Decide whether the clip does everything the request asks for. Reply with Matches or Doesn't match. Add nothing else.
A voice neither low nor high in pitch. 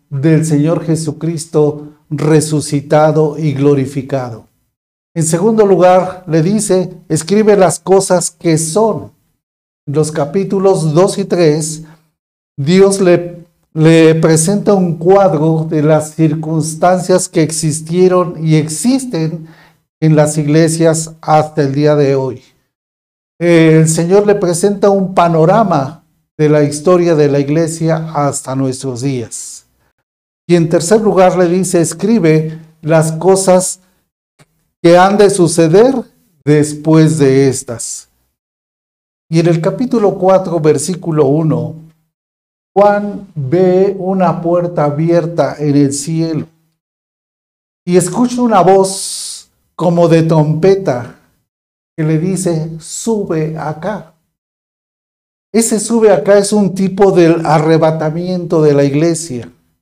Matches